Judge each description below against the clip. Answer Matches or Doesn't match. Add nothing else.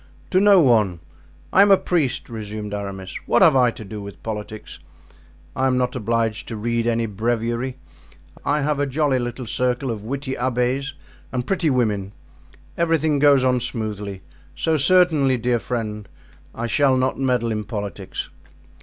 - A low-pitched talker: Matches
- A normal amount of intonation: Matches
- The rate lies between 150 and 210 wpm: Matches